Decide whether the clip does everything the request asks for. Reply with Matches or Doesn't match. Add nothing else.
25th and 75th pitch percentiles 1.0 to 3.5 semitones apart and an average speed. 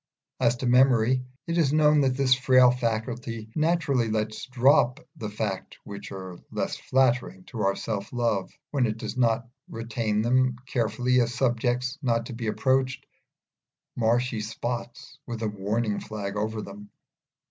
Matches